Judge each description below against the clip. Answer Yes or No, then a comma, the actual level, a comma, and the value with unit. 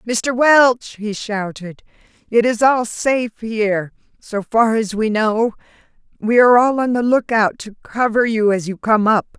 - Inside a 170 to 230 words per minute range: Yes, average, 175 wpm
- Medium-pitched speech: No, high, 225 Hz